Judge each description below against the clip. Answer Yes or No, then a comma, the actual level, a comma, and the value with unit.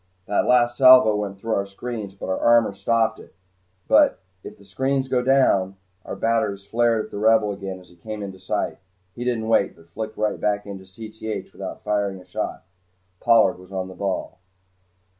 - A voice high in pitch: No, low, 105 Hz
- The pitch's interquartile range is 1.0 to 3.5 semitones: Yes, average, 2.9 semitones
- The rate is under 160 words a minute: No, average, 195 wpm